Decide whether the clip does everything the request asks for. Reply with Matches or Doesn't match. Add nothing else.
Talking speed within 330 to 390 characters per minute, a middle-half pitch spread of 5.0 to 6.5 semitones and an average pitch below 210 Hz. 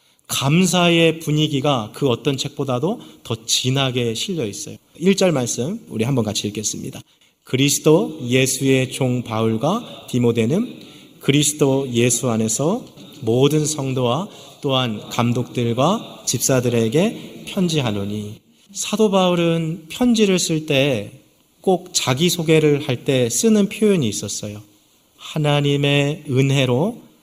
Doesn't match